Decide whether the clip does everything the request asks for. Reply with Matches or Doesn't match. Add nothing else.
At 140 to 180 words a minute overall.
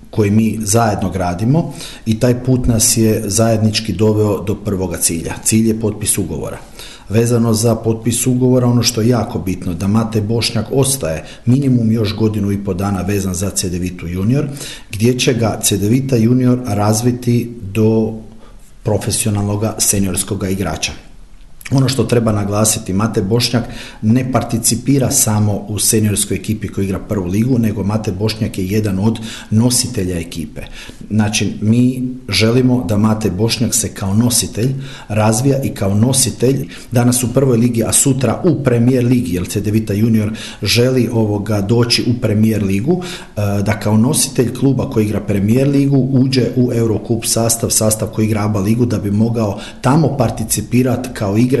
Matches